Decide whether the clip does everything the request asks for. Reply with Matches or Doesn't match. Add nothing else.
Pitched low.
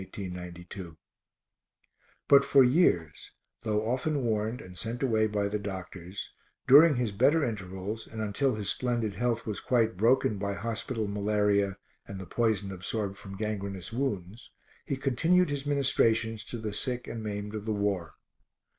Matches